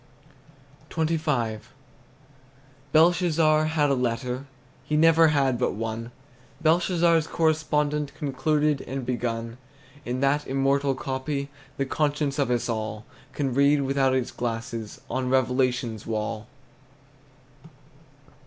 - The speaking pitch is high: No, low, 135 Hz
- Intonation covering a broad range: No, average, 3.7 semitones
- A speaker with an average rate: No, slow, 105 wpm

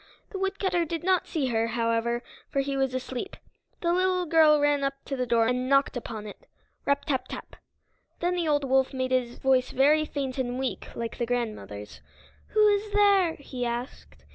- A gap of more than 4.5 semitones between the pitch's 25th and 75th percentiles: Yes, average, 5.1 semitones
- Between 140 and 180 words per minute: No, average, 190 wpm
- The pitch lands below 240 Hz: No, very high, 270 Hz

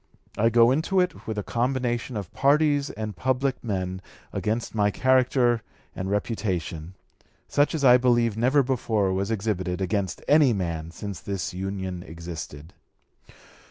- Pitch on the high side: No, low, 110 Hz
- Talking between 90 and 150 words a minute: Yes, average, 140 wpm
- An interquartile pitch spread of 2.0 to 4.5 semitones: No, average, 5.3 semitones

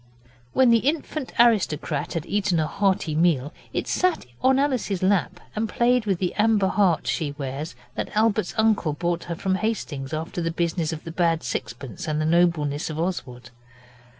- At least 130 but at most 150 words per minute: No, average, 175 wpm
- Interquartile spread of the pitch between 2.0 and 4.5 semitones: No, wide, 5.6 semitones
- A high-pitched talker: No, medium, 175 Hz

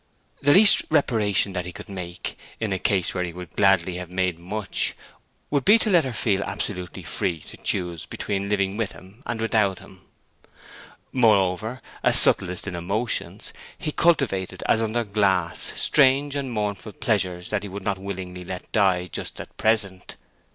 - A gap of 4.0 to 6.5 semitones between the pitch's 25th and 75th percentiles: No, average, 3.6 semitones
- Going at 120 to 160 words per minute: No, average, 170 wpm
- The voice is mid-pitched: No, low, 100 Hz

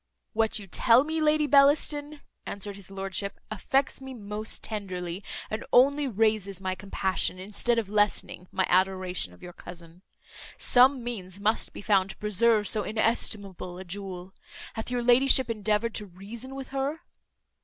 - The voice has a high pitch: Yes, high, 210 Hz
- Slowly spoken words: No, average, 155 wpm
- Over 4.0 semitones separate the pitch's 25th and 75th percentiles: Yes, average, 4.4 semitones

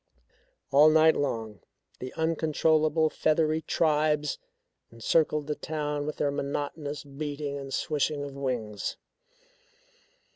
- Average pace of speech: No, slow, 105 wpm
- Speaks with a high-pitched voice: No, medium, 150 Hz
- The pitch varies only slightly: Yes, narrow, 1.8 semitones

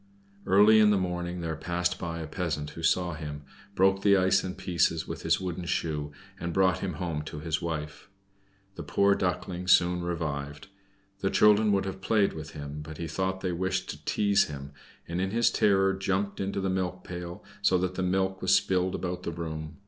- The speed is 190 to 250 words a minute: Yes, average, 200 wpm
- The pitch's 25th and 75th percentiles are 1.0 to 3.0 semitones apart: Yes, average, 2.7 semitones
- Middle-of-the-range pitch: No, very low, 90 Hz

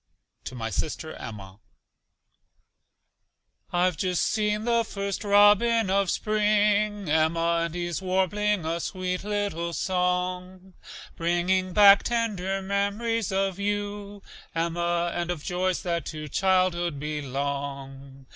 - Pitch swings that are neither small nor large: Yes, average, 3.3 semitones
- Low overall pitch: No, medium, 185 Hz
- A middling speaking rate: No, slow, 110 wpm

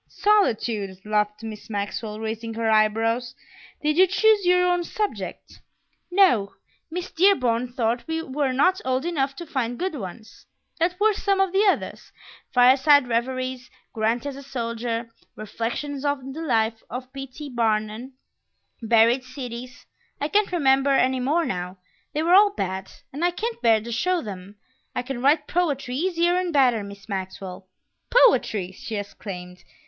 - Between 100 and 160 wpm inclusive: Yes, average, 155 wpm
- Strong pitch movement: Yes, wide, 6.5 semitones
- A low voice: No, very high, 255 Hz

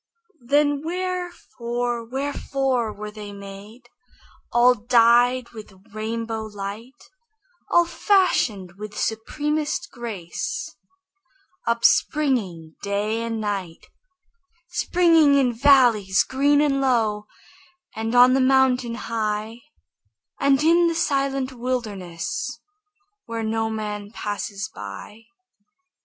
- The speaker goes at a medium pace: No, slow, 95 wpm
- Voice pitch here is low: No, high, 235 Hz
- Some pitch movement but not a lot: Yes, average, 4.5 semitones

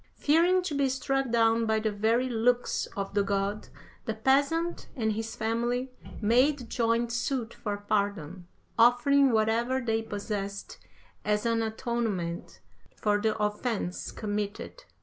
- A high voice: Yes, high, 225 Hz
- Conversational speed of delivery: No, slow, 130 wpm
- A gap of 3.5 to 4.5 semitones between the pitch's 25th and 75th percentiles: No, average, 3.0 semitones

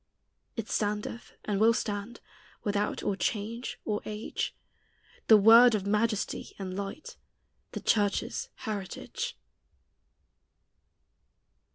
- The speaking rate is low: Yes, slow, 95 wpm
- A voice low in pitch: No, high, 210 Hz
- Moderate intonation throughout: No, narrow, 2.2 semitones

